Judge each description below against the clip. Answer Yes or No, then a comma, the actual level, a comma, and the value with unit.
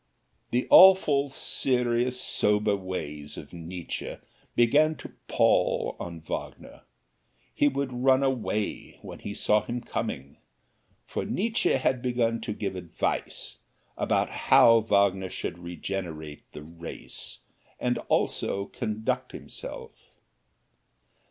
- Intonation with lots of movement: Yes, wide, 6.1 semitones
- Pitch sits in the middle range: No, low, 110 Hz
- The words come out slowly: Yes, slow, 110 wpm